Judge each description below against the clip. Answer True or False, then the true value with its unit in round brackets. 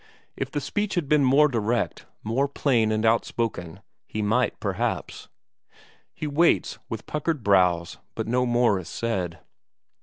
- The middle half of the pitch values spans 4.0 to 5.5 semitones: True (5.2 semitones)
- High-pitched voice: False (115 Hz)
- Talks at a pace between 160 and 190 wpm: False (145 wpm)